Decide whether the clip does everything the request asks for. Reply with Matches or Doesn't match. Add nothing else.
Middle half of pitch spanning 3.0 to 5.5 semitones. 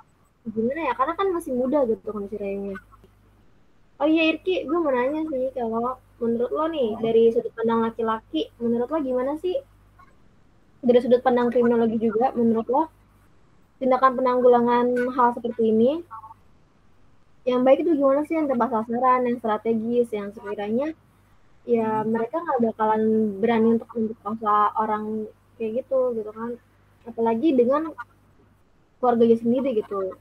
Doesn't match